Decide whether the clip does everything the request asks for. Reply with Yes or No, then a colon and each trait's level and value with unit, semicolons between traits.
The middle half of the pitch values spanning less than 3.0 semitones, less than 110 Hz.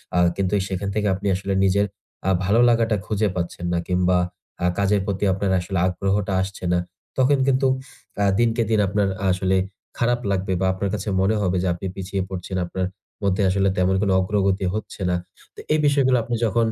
Yes: narrow, 2.4 semitones; low, 100 Hz